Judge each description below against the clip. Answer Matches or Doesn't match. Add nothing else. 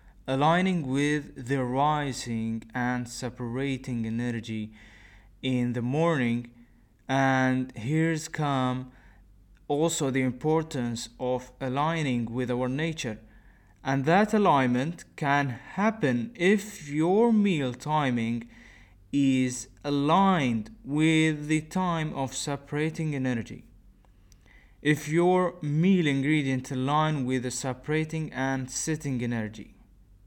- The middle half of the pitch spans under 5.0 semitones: Matches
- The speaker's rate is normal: Doesn't match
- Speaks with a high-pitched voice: Doesn't match